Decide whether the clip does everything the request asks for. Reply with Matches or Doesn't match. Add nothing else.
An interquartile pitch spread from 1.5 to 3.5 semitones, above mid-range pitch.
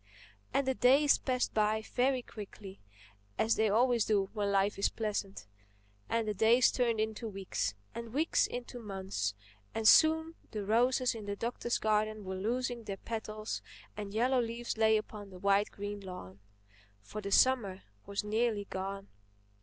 Matches